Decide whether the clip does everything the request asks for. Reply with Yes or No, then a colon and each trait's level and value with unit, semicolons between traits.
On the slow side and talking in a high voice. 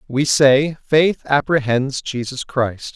No: slow, 120 wpm; low, 135 Hz